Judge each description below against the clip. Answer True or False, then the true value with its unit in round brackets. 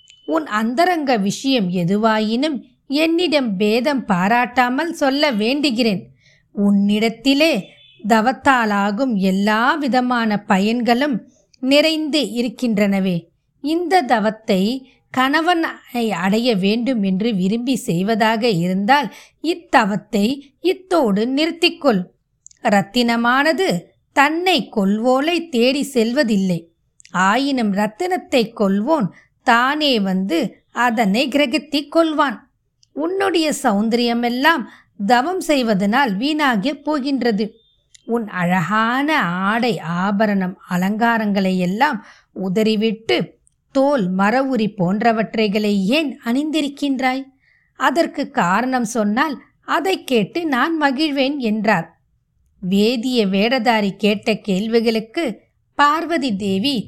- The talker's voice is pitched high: True (235 Hz)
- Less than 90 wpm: True (80 wpm)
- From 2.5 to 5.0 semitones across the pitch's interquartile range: False (5.5 semitones)